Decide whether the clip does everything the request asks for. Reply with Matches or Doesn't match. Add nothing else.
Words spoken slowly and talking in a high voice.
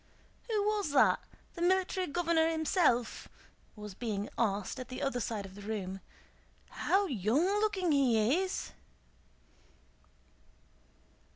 Matches